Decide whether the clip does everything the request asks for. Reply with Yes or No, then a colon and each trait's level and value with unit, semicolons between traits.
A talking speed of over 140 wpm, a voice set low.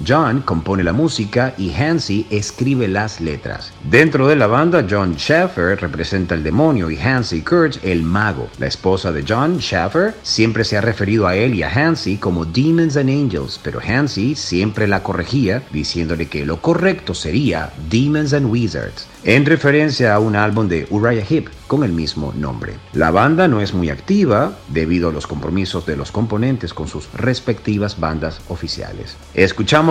Yes: average, 170 wpm; low, 105 Hz